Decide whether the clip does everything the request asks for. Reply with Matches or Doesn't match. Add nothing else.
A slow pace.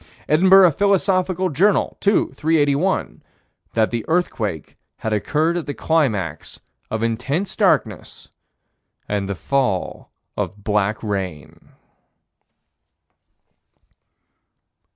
Matches